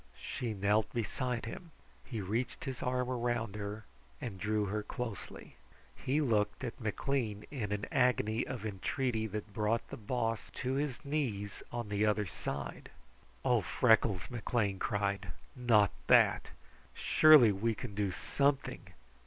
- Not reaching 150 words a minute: Yes, average, 140 wpm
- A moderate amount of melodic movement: Yes, average, 3.3 semitones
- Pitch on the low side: Yes, low, 110 Hz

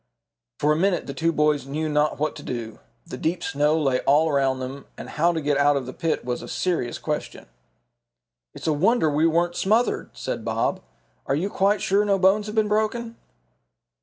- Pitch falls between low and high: Yes, medium, 155 Hz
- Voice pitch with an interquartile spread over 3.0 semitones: Yes, average, 5.1 semitones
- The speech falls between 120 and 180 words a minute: No, average, 200 wpm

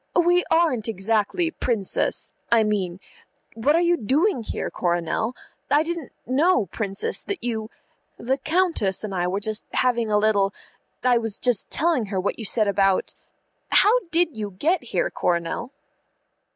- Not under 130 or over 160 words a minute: Yes, average, 150 wpm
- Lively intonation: Yes, wide, 7.6 semitones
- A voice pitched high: Yes, high, 230 Hz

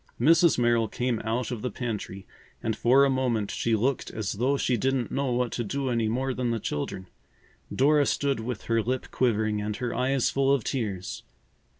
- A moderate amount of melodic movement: Yes, average, 3.1 semitones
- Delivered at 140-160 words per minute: No, average, 195 wpm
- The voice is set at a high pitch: No, low, 120 Hz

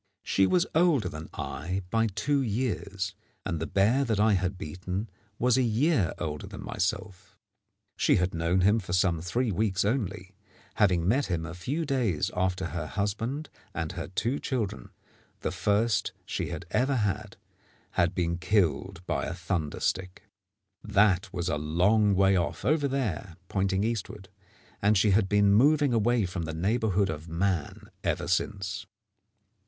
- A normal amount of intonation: Yes, average, 3.9 semitones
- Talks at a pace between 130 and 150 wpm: No, average, 160 wpm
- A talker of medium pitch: No, low, 100 Hz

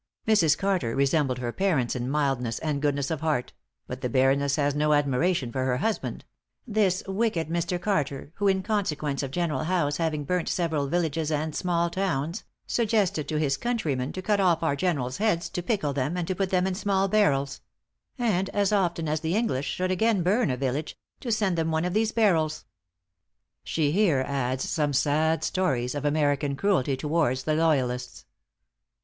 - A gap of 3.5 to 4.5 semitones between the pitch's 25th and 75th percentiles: No, average, 5.1 semitones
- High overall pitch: No, medium, 160 Hz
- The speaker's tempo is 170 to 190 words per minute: Yes, average, 180 wpm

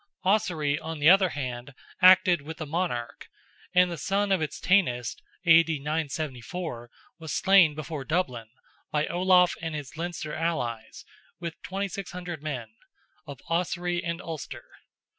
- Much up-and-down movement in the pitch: No, average, 3.7 semitones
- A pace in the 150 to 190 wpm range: No, slow, 135 wpm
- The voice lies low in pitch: No, medium, 165 Hz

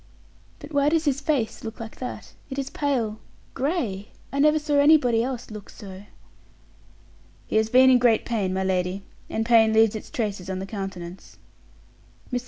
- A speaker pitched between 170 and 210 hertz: No, high, 225 Hz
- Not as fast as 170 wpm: No, average, 175 wpm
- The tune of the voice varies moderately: No, wide, 5.7 semitones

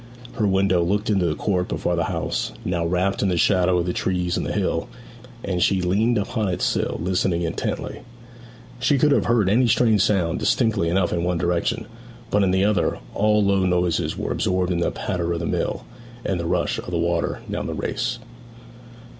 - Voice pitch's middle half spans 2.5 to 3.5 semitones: Yes, average, 2.8 semitones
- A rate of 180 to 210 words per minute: Yes, average, 195 wpm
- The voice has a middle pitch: No, very low, 95 Hz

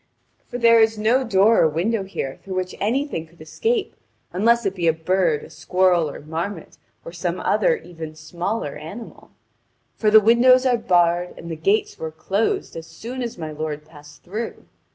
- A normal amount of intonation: No, wide, 6.1 semitones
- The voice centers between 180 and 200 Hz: Yes, medium, 185 Hz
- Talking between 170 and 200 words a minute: Yes, average, 180 wpm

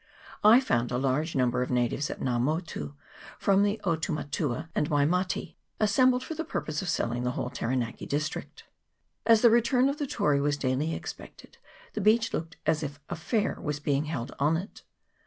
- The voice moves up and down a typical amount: No, wide, 7.2 semitones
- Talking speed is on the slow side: No, average, 190 wpm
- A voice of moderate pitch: Yes, medium, 155 Hz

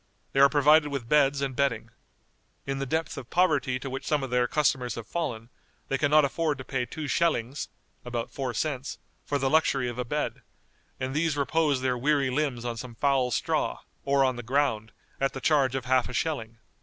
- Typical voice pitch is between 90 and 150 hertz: Yes, low, 135 Hz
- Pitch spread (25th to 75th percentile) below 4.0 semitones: Yes, average, 2.8 semitones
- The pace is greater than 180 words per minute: Yes, fast, 205 wpm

